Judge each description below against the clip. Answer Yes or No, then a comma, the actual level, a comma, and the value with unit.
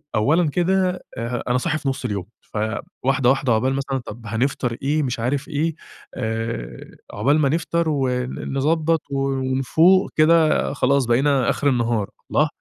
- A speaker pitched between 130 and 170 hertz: Yes, low, 135 Hz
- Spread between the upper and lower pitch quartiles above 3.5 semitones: Yes, average, 4.1 semitones